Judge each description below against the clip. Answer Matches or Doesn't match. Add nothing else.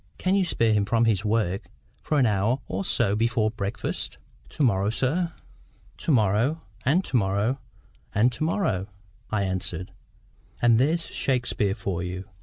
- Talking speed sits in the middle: Matches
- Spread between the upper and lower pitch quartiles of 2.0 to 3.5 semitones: Doesn't match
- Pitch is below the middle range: Matches